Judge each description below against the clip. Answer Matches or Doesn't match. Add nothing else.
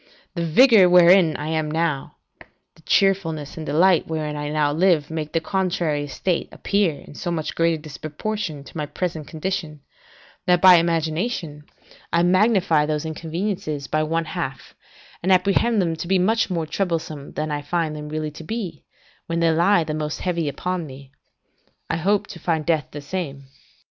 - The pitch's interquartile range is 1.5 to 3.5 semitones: Matches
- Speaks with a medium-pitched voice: Matches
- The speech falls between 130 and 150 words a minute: Doesn't match